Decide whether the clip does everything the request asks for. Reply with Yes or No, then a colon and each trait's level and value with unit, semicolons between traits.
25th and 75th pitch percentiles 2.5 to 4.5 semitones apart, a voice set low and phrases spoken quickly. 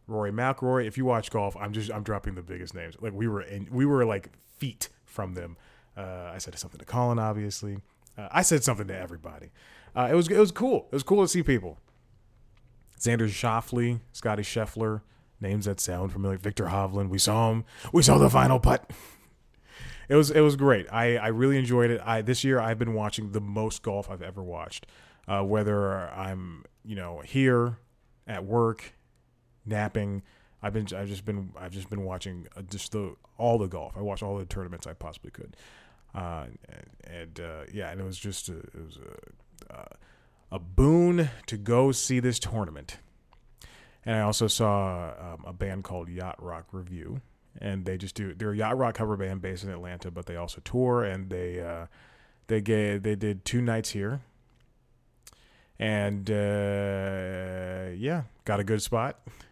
No: average, 4.0 semitones; low, 105 Hz; average, 185 wpm